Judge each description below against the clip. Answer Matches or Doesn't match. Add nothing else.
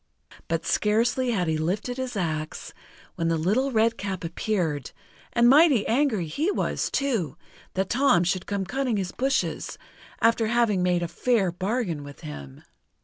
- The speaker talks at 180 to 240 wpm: Doesn't match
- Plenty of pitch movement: Matches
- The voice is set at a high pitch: Matches